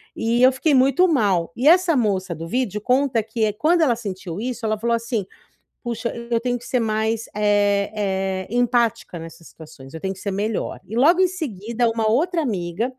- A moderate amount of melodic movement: Yes, average, 4.0 semitones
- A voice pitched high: Yes, high, 225 Hz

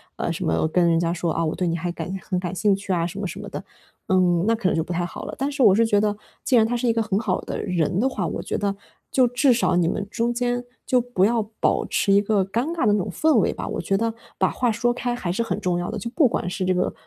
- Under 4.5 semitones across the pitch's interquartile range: No, average, 4.8 semitones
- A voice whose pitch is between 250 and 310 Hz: No, high, 205 Hz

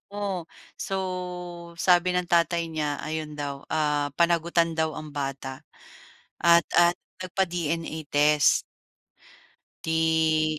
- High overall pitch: No, medium, 160 Hz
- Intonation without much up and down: Yes, narrow, 2.3 semitones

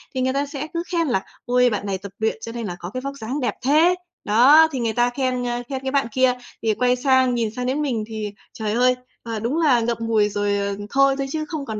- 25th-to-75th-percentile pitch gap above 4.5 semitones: No, average, 3.7 semitones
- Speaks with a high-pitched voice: Yes, very high, 250 Hz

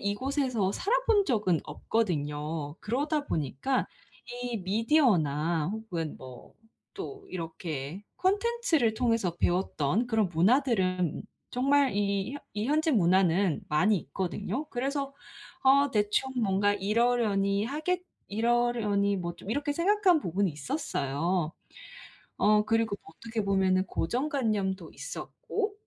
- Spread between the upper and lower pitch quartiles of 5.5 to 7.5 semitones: Yes, wide, 6.7 semitones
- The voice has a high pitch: Yes, high, 210 Hz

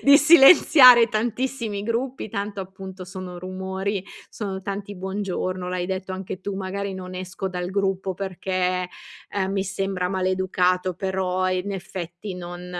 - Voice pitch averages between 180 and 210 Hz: Yes, high, 190 Hz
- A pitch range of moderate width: No, narrow, 1.5 semitones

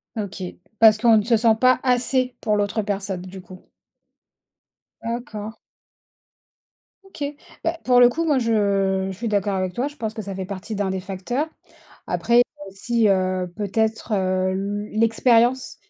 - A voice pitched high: Yes, high, 215 Hz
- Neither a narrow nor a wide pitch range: Yes, average, 3.7 semitones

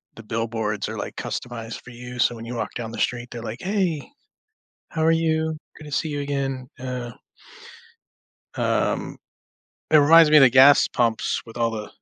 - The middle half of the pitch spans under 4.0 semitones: No, average, 4.6 semitones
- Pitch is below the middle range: Yes, low, 125 Hz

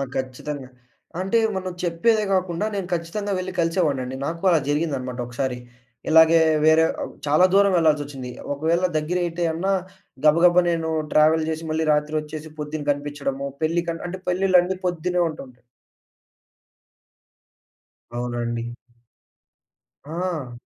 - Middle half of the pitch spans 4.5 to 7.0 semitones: No, average, 3.4 semitones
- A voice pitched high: No, medium, 160 Hz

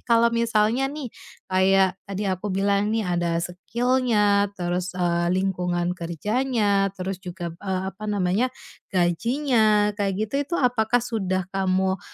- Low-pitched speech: No, high, 200 Hz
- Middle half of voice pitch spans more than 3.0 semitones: Yes, average, 3.7 semitones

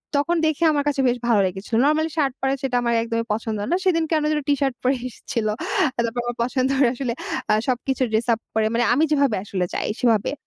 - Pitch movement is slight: No, average, 3.7 semitones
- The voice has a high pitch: Yes, very high, 255 Hz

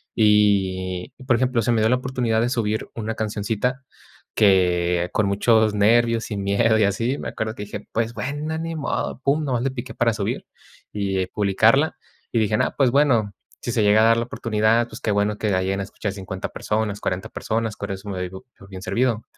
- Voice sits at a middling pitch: No, low, 110 Hz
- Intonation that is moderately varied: Yes, average, 3.0 semitones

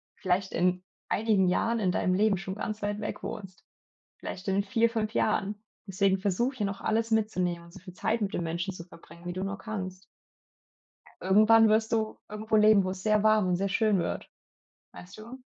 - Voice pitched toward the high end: Yes, high, 200 Hz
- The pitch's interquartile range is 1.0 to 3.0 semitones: Yes, average, 2.7 semitones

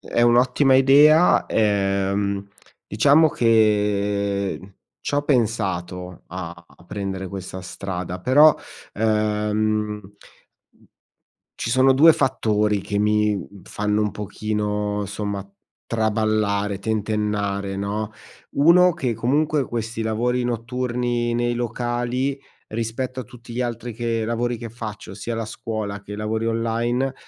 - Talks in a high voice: No, low, 110 Hz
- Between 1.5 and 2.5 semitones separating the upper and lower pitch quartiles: No, average, 2.9 semitones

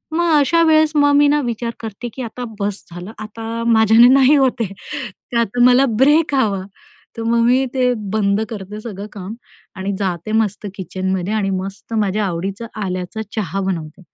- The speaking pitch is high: Yes, high, 220 Hz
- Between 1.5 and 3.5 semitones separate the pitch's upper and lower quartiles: No, average, 4.2 semitones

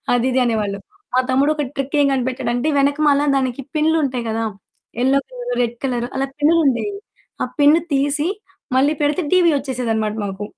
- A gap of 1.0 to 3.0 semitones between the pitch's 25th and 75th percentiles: No, average, 3.4 semitones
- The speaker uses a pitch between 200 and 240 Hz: No, very high, 270 Hz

